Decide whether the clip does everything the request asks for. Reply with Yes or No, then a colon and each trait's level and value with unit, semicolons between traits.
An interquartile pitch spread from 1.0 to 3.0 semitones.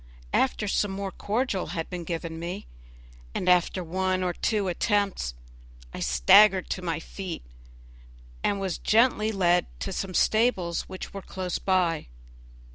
Yes: narrow, 2.6 semitones